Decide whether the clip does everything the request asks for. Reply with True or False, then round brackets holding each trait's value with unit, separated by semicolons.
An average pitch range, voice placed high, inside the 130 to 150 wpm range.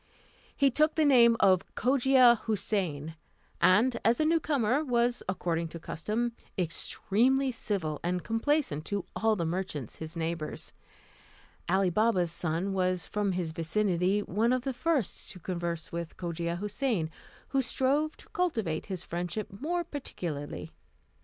False (6.5 semitones; 200 Hz; 140 wpm)